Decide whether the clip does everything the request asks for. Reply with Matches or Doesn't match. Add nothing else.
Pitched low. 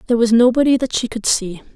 Doesn't match